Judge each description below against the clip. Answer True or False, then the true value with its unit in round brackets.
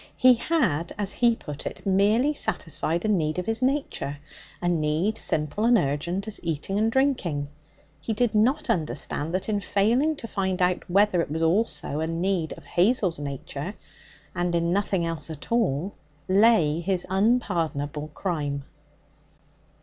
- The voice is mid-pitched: True (180 Hz)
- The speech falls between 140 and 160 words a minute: True (155 wpm)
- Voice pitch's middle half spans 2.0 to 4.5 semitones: False (5.5 semitones)